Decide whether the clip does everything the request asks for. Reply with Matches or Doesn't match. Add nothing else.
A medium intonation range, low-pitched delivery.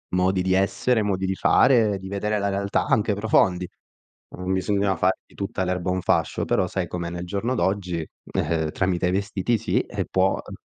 Doesn't match